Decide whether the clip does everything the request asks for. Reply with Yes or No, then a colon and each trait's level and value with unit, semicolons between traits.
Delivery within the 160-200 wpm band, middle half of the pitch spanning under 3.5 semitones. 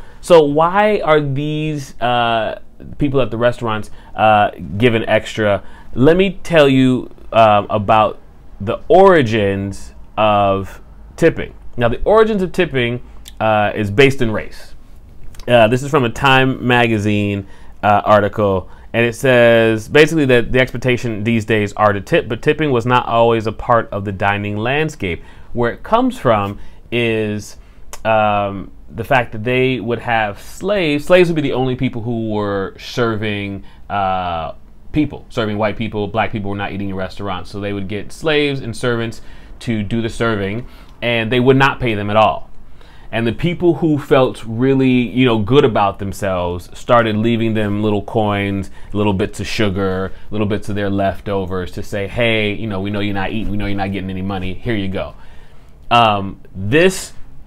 No: average, 170 wpm; average, 3.9 semitones